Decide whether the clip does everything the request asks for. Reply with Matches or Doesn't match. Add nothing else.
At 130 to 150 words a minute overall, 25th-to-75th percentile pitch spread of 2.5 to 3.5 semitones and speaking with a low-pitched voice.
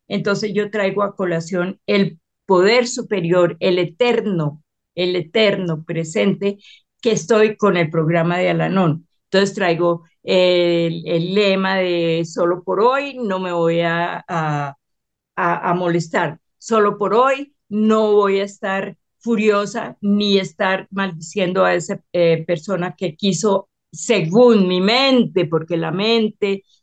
Doesn't match